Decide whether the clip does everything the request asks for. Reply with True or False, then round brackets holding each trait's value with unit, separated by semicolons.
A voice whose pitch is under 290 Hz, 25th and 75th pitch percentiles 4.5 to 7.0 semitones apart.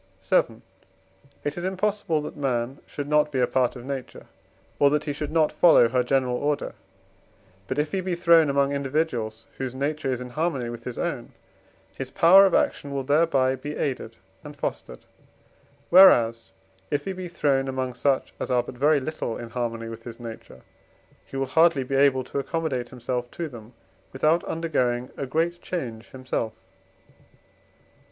False (135 Hz; 3.9 semitones)